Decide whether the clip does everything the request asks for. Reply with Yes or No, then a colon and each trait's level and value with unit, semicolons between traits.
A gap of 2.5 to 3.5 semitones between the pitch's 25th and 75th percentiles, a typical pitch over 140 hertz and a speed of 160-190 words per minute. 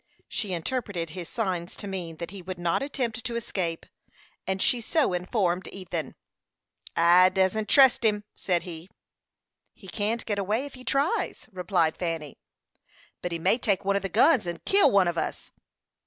No: average, 4.3 semitones; high, 190 Hz; average, 170 wpm